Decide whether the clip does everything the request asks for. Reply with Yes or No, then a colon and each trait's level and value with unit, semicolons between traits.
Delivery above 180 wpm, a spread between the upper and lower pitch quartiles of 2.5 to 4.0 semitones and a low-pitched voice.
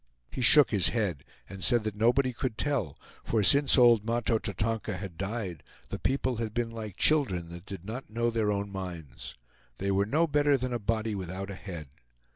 Yes: average, 195 wpm; average, 3.7 semitones; low, 110 Hz